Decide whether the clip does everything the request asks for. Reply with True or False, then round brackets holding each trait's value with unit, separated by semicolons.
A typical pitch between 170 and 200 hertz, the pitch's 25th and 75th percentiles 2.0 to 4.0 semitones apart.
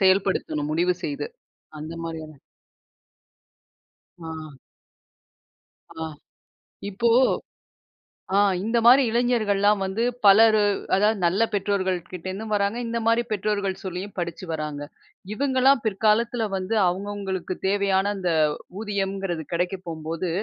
True (195 Hz; 3.3 semitones)